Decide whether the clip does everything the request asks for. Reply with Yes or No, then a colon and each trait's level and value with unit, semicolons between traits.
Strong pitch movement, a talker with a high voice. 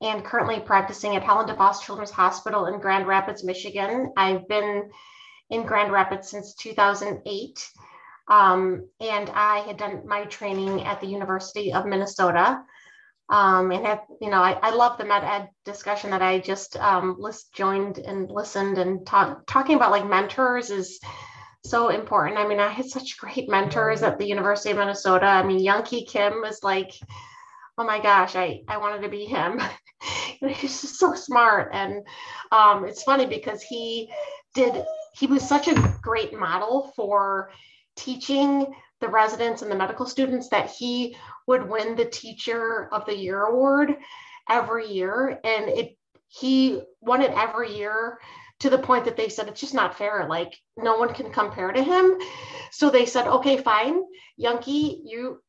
No: average, 4.5 semitones; high, 215 Hz